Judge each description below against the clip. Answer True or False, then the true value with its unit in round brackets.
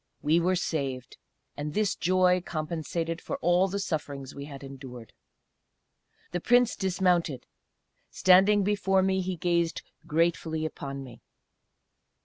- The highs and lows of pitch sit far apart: False (4.2 semitones)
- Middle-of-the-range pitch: True (170 Hz)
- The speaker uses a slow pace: True (125 wpm)